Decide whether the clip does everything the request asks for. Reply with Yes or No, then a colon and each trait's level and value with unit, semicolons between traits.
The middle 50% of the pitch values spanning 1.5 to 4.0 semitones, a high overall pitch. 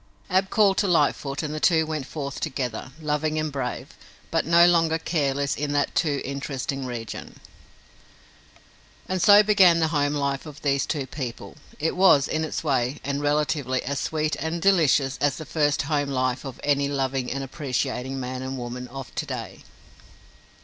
No: average, 2.8 semitones; medium, 145 Hz